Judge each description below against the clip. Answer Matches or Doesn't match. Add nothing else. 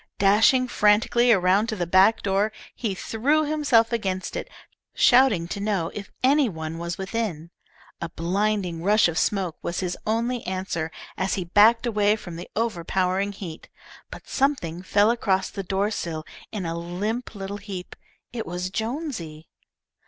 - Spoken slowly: Doesn't match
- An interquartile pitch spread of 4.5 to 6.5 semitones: Doesn't match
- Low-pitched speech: Doesn't match